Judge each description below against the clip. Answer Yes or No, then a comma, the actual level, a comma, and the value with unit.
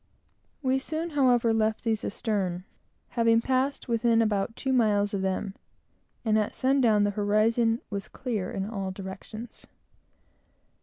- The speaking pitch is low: No, high, 225 Hz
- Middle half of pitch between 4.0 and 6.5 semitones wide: No, average, 3.0 semitones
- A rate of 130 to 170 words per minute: Yes, slow, 135 wpm